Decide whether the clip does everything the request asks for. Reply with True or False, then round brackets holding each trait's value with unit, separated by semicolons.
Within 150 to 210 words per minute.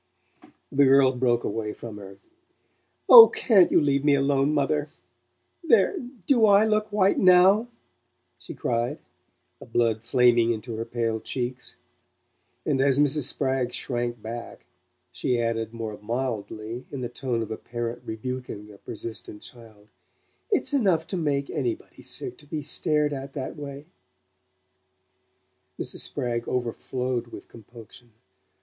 False (135 wpm)